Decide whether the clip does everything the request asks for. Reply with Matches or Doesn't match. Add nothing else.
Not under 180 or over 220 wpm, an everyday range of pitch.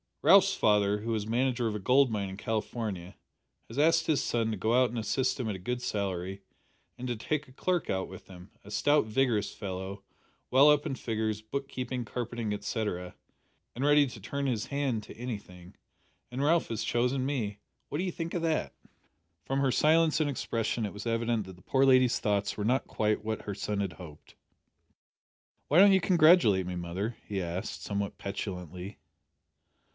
Matches